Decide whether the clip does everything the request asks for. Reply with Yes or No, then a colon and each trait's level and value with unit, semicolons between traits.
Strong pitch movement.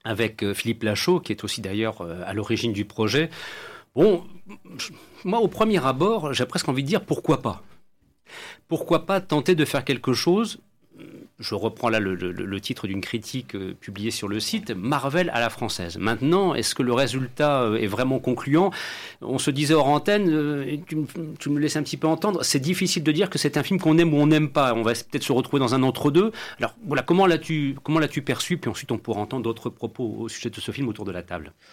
Yes: wide, 5.9 semitones